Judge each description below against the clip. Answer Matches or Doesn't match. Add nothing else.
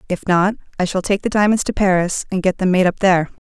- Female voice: Matches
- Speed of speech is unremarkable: Doesn't match